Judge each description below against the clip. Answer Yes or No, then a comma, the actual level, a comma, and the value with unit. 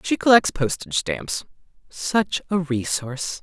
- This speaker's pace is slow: Yes, slow, 120 wpm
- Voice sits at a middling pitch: Yes, medium, 145 Hz